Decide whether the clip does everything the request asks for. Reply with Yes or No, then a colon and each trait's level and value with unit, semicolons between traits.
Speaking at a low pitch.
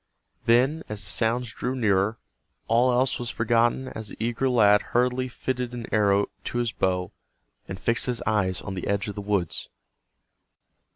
Yes: low, 115 Hz